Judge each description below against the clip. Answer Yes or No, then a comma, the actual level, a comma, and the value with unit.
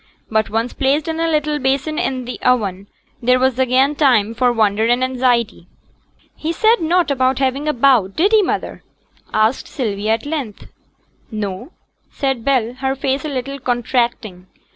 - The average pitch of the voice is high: Yes, very high, 255 Hz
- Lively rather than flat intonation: No, average, 3.6 semitones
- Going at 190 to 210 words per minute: No, average, 165 wpm